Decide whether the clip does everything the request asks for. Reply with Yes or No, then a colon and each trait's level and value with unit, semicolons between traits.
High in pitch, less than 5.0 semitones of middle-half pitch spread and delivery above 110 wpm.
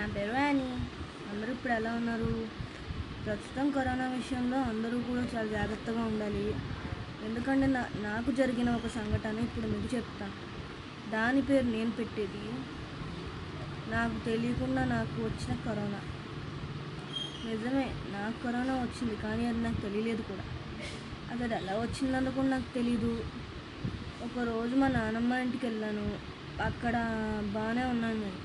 Yes: high, 230 Hz; average, 2.9 semitones; average, 120 wpm